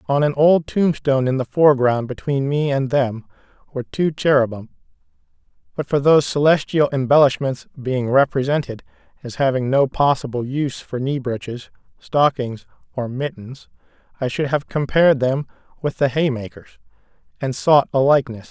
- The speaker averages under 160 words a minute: Yes, average, 145 wpm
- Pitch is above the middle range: No, low, 135 Hz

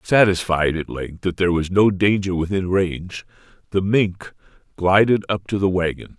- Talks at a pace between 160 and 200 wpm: Yes, average, 165 wpm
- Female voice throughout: No, male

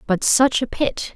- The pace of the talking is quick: Yes, fast, 210 wpm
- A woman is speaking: Yes, female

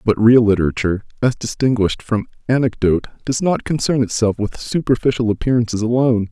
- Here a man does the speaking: Yes, male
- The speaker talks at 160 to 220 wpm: No, average, 145 wpm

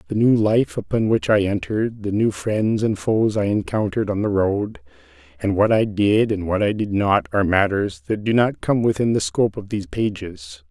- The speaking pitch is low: Yes, low, 105 Hz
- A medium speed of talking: No, fast, 215 wpm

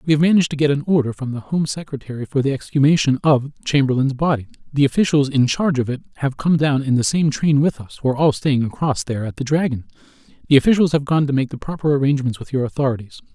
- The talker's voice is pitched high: No, medium, 140 Hz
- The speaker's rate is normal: No, fast, 235 wpm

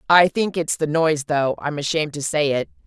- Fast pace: Yes, fast, 230 wpm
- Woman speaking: Yes, female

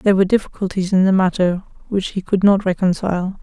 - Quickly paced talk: No, average, 195 wpm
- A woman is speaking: Yes, female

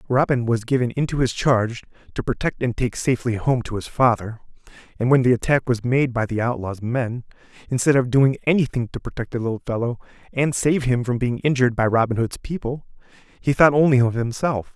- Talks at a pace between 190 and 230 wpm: Yes, average, 200 wpm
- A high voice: No, low, 125 Hz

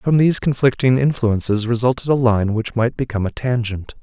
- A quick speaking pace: No, average, 180 wpm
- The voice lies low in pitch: Yes, low, 120 Hz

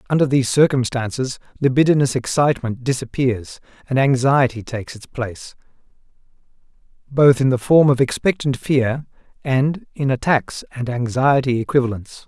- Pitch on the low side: Yes, low, 130 Hz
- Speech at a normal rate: No, slow, 115 wpm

